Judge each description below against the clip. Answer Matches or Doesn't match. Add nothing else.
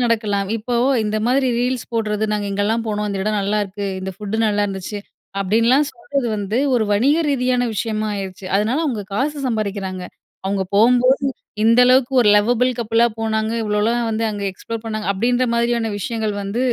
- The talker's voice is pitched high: Matches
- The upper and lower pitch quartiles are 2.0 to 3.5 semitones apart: Matches